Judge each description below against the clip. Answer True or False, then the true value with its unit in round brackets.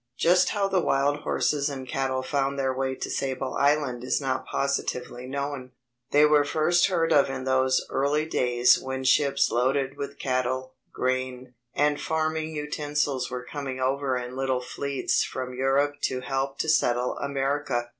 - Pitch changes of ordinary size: False (2.0 semitones)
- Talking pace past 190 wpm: False (160 wpm)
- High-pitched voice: False (135 Hz)